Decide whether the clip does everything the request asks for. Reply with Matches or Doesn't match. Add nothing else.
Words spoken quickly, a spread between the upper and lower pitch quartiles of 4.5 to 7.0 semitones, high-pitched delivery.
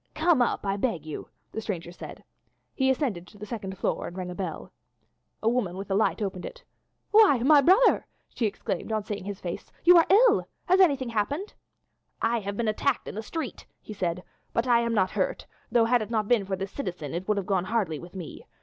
Matches